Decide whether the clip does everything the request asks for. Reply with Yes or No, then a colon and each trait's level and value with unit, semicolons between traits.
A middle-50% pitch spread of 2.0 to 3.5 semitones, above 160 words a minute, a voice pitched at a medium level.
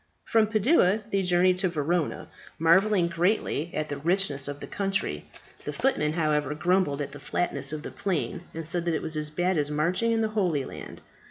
No: average, 4.2 semitones; average, 195 wpm; medium, 170 Hz